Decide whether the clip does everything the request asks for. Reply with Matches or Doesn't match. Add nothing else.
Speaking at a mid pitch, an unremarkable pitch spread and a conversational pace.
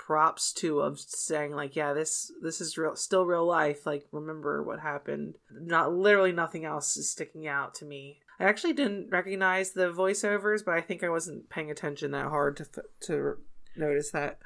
Matches